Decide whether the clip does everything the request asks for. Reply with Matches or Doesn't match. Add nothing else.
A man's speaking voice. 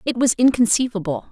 Doesn't match